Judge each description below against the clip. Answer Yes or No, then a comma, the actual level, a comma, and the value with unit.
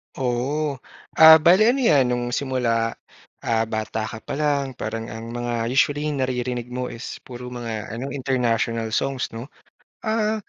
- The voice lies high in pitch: No, low, 125 Hz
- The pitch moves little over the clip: No, average, 3.5 semitones